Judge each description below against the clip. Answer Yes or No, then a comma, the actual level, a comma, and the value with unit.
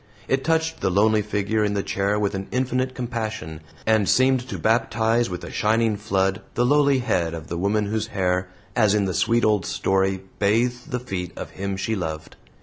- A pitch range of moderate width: Yes, average, 3.7 semitones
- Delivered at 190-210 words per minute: Yes, average, 195 wpm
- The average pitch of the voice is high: No, low, 105 Hz